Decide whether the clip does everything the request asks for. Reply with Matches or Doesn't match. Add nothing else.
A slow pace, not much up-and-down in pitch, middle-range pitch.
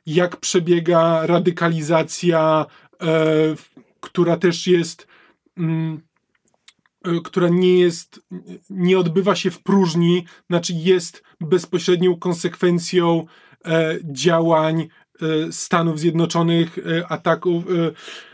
Matches